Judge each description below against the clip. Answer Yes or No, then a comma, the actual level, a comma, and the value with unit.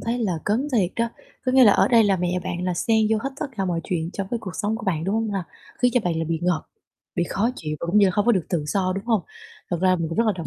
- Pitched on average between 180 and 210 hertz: Yes, high, 195 Hz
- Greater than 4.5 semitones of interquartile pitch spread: No, average, 4.2 semitones